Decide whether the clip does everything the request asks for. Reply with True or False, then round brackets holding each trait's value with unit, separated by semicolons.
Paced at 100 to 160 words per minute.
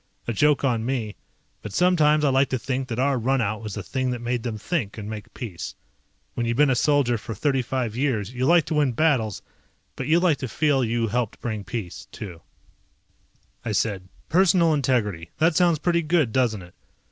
False (200 wpm)